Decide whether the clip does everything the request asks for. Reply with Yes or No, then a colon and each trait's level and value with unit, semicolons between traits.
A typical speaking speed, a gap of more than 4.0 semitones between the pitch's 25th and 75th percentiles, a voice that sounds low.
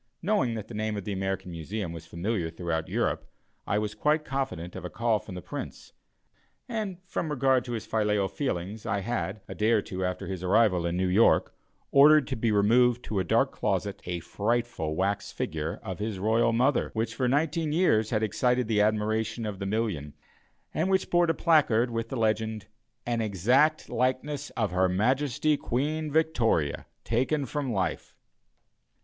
Yes: average, 180 wpm; average, 5.0 semitones; low, 110 Hz